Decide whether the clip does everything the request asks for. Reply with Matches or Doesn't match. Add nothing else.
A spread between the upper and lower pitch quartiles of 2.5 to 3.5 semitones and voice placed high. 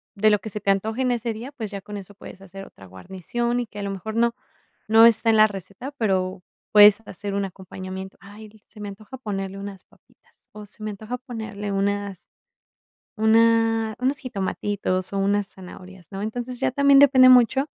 Matches